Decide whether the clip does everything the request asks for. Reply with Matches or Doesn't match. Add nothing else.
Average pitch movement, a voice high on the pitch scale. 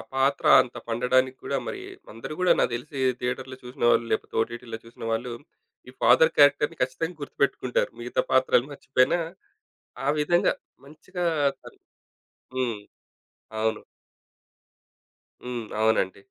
Doesn't match